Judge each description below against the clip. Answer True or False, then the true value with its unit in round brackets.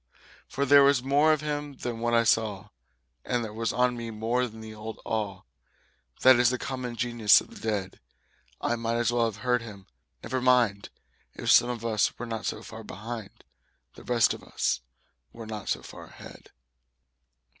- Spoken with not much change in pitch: True (2.2 semitones)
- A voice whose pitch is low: True (115 Hz)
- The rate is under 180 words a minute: False (185 wpm)